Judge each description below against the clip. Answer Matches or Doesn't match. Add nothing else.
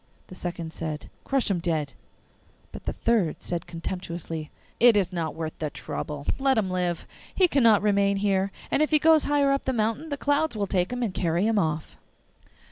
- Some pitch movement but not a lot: Doesn't match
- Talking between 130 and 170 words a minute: Doesn't match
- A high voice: Matches